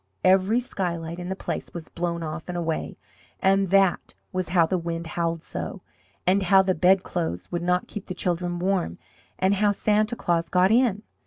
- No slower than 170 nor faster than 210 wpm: Yes, average, 180 wpm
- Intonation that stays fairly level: Yes, narrow, 2.3 semitones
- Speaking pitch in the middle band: Yes, medium, 180 Hz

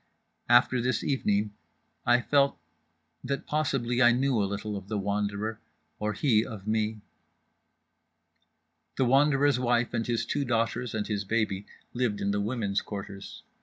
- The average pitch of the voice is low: Yes, low, 115 Hz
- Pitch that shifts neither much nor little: Yes, average, 3.4 semitones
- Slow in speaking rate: No, average, 145 wpm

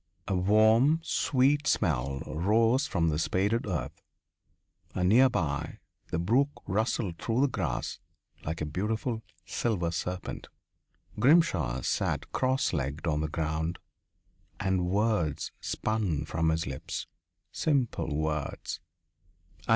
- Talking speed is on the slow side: Yes, slow, 115 wpm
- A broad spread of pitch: Yes, wide, 6.6 semitones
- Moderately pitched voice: No, very low, 95 Hz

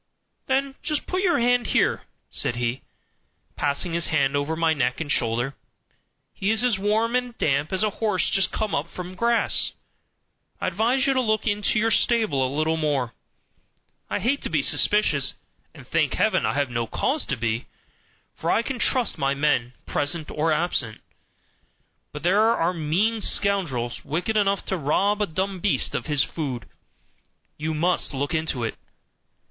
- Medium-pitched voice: Yes, medium, 170 Hz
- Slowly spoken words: No, average, 170 wpm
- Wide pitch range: Yes, wide, 7.2 semitones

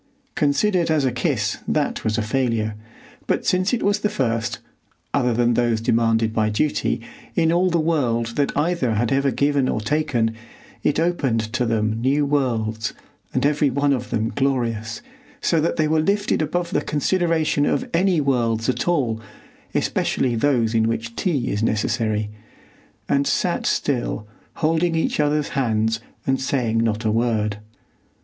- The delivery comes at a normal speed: Yes, average, 160 wpm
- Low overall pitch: Yes, low, 130 Hz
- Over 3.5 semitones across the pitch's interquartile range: Yes, average, 5.2 semitones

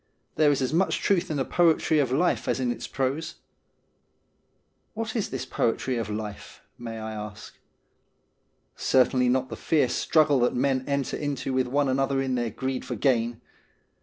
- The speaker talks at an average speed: Yes, average, 175 wpm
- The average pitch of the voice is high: No, low, 130 Hz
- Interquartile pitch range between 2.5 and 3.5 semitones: Yes, average, 2.9 semitones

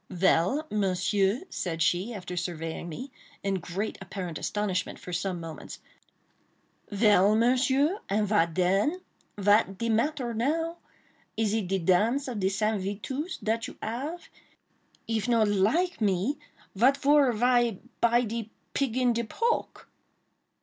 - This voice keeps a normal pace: No, slow, 130 wpm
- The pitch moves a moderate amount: Yes, average, 4.7 semitones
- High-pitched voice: Yes, high, 215 Hz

